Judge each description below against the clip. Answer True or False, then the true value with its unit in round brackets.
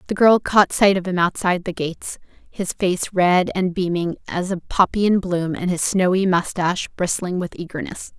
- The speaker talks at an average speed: True (190 wpm)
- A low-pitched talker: False (180 Hz)